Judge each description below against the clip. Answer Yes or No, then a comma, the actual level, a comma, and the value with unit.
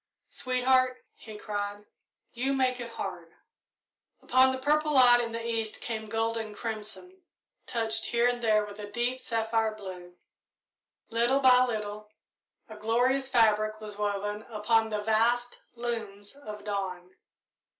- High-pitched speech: Yes, high, 225 Hz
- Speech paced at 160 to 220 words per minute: No, slow, 135 wpm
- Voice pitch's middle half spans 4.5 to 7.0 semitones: No, average, 2.7 semitones